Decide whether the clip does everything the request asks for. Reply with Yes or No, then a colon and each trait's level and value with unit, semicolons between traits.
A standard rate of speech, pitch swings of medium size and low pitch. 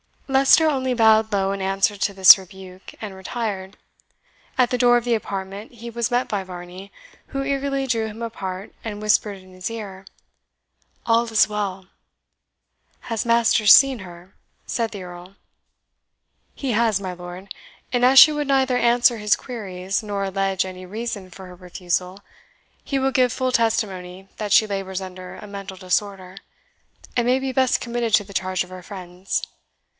No: average, 170 wpm; average, 4.0 semitones; high, 205 Hz